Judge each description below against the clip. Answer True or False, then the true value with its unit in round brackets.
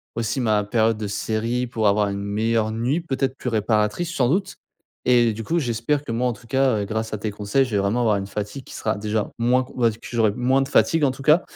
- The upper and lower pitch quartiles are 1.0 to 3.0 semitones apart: False (3.4 semitones)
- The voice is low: True (115 Hz)